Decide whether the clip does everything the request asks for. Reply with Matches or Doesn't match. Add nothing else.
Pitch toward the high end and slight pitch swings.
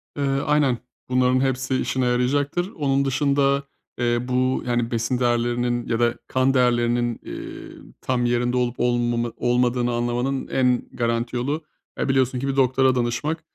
Doesn't match